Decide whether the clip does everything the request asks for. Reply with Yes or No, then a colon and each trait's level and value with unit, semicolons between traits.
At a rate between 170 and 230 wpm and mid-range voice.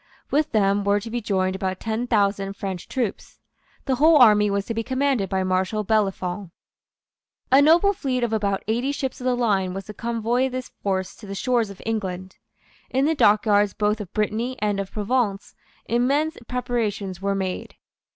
No: average, 180 wpm; high, 215 Hz